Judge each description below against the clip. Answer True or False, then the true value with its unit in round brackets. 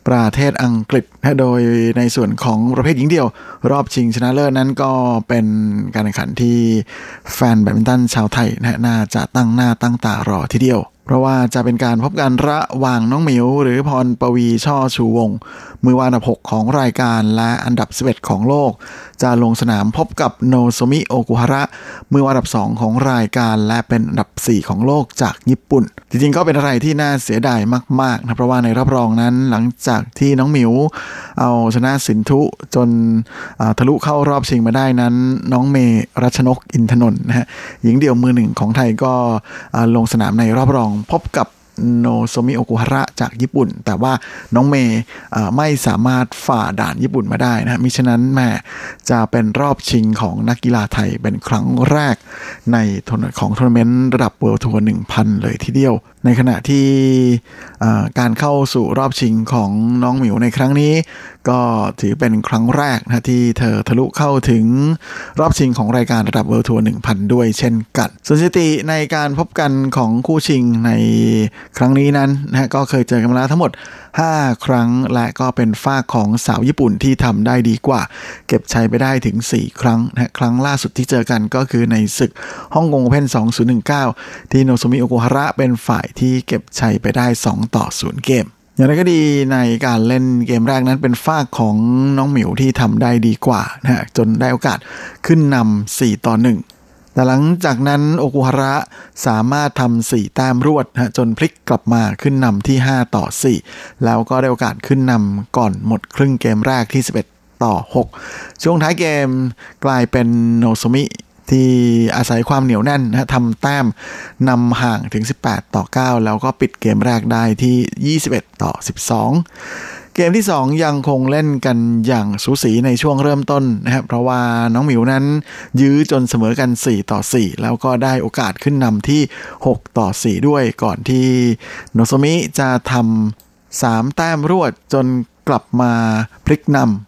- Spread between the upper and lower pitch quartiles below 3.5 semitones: True (2.5 semitones)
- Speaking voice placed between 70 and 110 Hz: False (125 Hz)